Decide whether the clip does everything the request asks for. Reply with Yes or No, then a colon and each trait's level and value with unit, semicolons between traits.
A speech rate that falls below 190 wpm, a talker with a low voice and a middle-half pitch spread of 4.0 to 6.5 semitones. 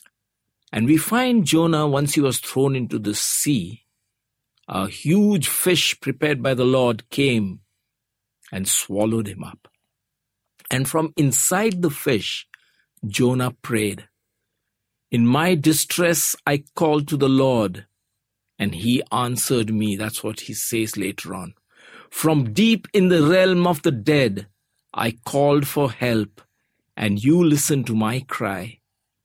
Yes: slow, 135 wpm; low, 125 Hz; wide, 5.6 semitones